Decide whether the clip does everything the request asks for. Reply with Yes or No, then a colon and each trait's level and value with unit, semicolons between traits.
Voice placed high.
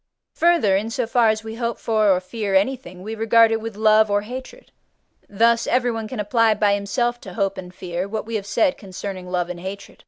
Yes: high, 215 Hz